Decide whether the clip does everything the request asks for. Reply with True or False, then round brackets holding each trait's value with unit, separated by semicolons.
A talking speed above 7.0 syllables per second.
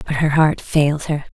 False (5.1 syllables/s)